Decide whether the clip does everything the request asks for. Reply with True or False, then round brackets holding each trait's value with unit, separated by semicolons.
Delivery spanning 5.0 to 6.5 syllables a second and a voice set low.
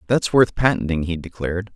True (5.8 syllables/s; 100 Hz)